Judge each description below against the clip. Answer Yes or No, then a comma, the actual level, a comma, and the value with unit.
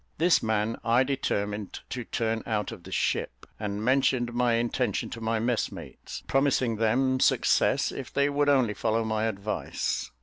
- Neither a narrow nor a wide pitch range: Yes, average, 3.0 semitones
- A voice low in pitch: Yes, low, 115 Hz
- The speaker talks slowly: No, average, 160 wpm